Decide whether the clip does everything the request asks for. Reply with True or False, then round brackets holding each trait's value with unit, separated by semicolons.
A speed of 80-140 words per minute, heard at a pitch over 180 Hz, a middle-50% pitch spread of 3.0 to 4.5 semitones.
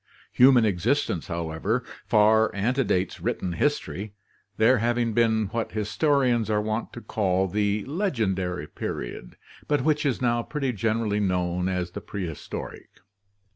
False (135 wpm; 110 Hz; 4.2 semitones)